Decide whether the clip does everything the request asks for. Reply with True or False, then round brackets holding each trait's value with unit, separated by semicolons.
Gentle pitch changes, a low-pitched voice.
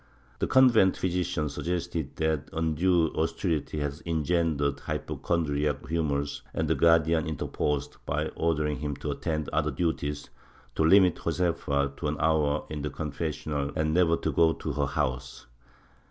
True (2.3 semitones; 80 Hz)